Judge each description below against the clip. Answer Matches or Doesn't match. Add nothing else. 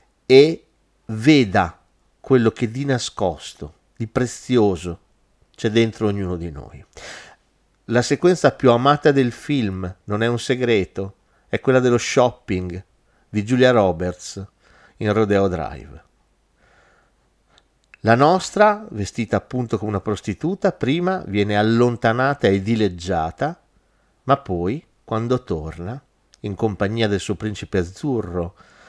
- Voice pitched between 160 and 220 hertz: Doesn't match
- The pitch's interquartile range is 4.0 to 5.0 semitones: Matches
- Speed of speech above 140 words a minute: Doesn't match